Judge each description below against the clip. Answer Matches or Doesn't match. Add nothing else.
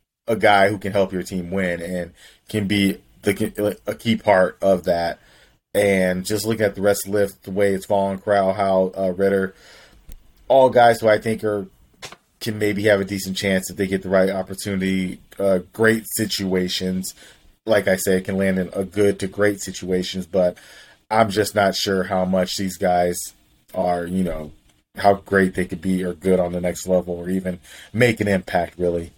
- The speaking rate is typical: Matches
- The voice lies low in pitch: Matches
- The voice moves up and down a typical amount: Doesn't match